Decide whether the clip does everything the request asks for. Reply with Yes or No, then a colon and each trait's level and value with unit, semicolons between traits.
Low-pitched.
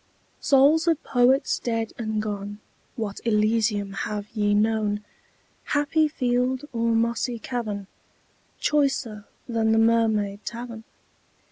No: high, 225 Hz